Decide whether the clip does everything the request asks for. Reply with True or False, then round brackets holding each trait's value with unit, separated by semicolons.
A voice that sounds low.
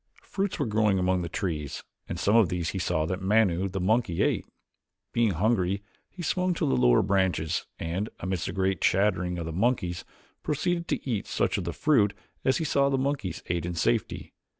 True (95 Hz)